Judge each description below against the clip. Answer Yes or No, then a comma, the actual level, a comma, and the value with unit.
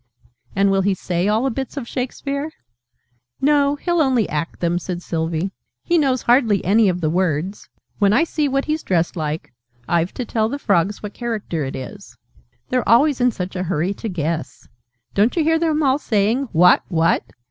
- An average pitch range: No, wide, 7.3 semitones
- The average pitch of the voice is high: Yes, high, 210 Hz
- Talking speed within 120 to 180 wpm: No, average, 190 wpm